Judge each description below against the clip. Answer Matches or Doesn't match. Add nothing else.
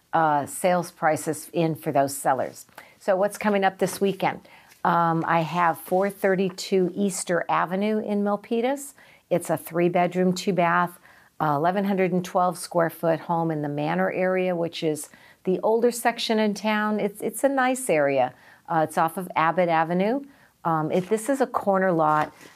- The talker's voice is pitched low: Doesn't match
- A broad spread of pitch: Doesn't match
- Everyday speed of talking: Matches